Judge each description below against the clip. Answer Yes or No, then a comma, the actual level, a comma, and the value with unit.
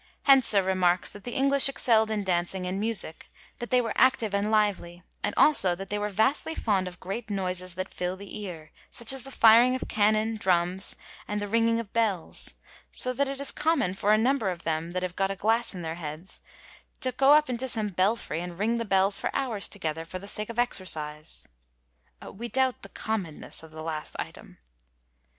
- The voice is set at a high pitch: Yes, high, 205 Hz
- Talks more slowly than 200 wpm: No, fast, 205 wpm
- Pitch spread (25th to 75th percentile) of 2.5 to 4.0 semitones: No, average, 4.4 semitones